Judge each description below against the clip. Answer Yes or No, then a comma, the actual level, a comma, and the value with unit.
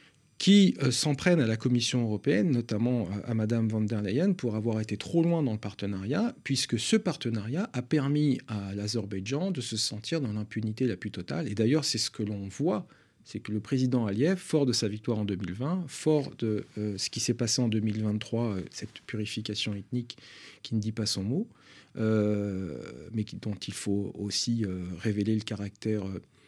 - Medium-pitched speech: No, low, 110 Hz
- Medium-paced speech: Yes, average, 195 wpm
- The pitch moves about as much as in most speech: Yes, average, 4.0 semitones